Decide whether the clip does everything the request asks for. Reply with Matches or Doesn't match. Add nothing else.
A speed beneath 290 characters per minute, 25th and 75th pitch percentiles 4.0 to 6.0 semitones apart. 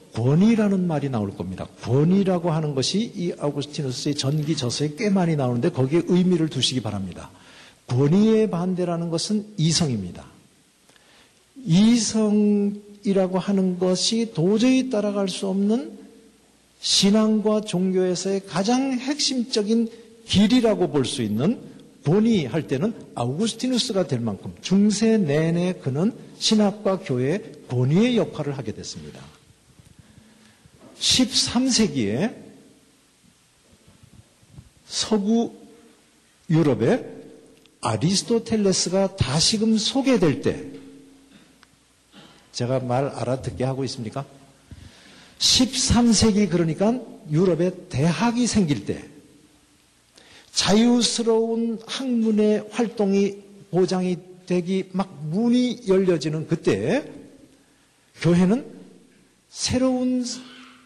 Doesn't match